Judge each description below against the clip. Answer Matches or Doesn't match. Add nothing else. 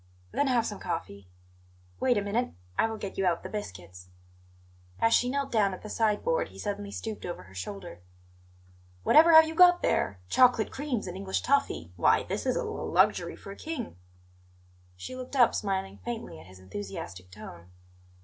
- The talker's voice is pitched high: Matches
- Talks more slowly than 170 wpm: Doesn't match